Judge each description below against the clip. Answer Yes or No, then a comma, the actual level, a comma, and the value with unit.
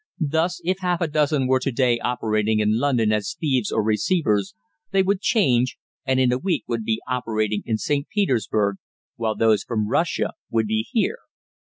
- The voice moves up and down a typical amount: No, wide, 5.8 semitones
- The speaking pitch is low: Yes, low, 125 Hz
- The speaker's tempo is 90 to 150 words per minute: No, average, 180 wpm